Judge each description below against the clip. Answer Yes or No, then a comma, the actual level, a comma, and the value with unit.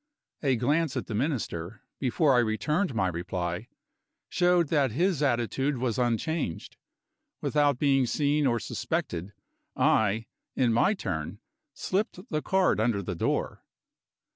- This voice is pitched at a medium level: No, low, 125 Hz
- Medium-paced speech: No, slow, 130 wpm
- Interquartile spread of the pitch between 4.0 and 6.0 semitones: Yes, wide, 5.6 semitones